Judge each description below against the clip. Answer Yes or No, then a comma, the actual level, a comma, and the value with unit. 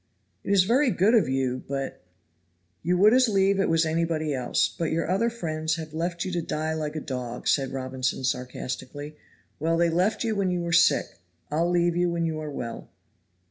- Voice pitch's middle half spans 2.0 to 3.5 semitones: No, average, 4.7 semitones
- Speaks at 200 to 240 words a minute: Yes, fast, 205 wpm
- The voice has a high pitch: No, medium, 160 Hz